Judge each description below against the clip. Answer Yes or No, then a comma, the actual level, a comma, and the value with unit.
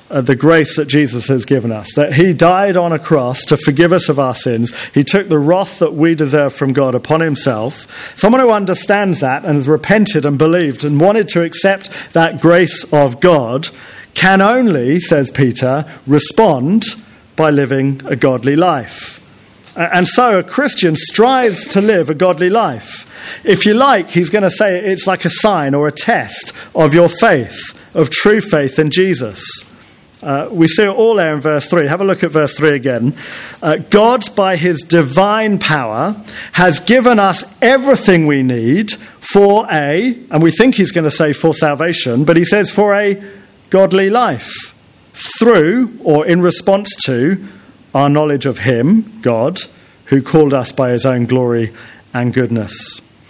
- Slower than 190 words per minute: Yes, average, 175 wpm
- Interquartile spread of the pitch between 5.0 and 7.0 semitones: Yes, wide, 5.6 semitones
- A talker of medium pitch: Yes, medium, 165 Hz